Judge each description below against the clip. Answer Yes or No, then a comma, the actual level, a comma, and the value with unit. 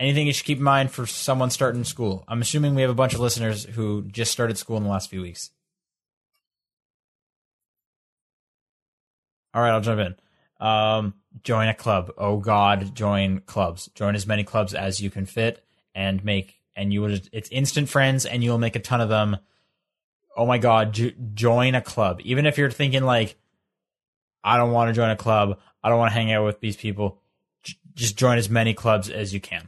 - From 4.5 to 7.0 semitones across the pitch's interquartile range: No, average, 3.2 semitones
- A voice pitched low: Yes, low, 110 Hz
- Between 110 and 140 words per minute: No, fast, 205 wpm